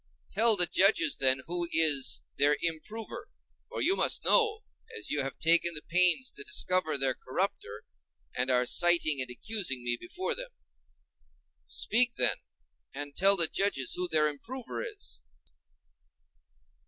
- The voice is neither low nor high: Yes, medium, 170 Hz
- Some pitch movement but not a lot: No, wide, 7.7 semitones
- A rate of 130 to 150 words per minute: Yes, average, 140 wpm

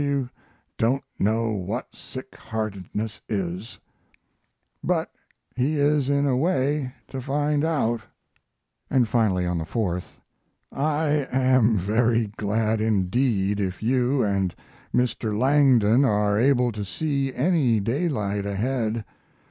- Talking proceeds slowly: Yes, slow, 115 wpm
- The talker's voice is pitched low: Yes, low, 115 Hz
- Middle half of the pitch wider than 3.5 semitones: Yes, average, 4.6 semitones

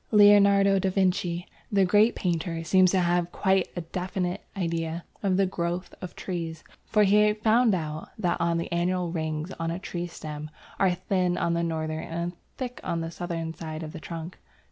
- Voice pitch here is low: No, medium, 175 Hz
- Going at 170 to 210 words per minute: Yes, average, 185 wpm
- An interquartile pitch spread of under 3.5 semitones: Yes, narrow, 2.5 semitones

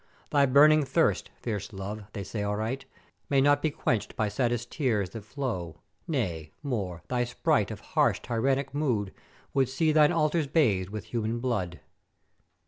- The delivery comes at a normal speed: Yes, average, 155 wpm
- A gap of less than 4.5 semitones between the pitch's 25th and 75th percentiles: No, average, 5.3 semitones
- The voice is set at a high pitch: No, low, 120 Hz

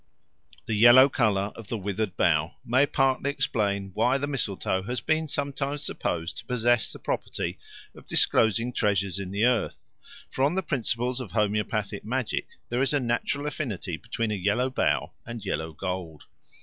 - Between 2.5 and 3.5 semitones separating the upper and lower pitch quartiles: No, average, 4.8 semitones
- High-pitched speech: No, low, 115 Hz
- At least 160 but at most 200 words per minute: Yes, average, 165 wpm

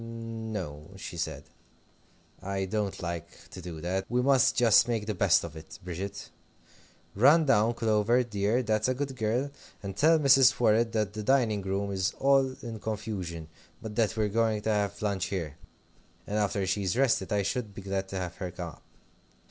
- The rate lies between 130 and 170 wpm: No, average, 185 wpm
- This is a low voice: Yes, low, 105 Hz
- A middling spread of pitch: Yes, average, 3.5 semitones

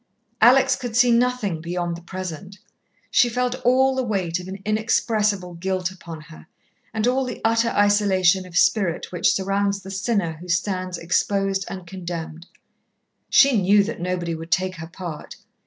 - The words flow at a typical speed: Yes, average, 160 wpm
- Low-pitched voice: No, high, 190 Hz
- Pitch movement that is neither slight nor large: Yes, average, 3.9 semitones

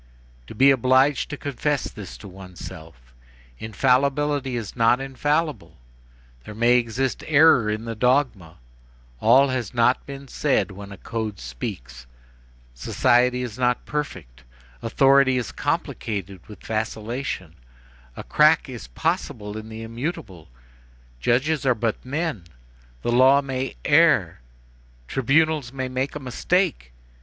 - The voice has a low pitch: Yes, low, 125 Hz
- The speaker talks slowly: Yes, slow, 125 wpm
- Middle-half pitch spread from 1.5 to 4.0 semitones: No, average, 4.5 semitones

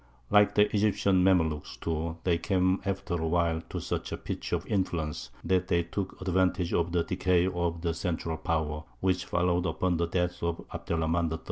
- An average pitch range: No, narrow, 1.9 semitones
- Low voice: Yes, very low, 85 Hz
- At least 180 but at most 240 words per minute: Yes, average, 195 wpm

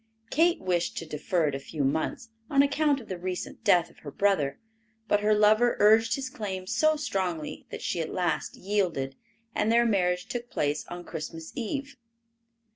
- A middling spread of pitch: No, wide, 6.0 semitones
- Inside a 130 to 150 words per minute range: No, average, 180 wpm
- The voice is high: Yes, high, 195 Hz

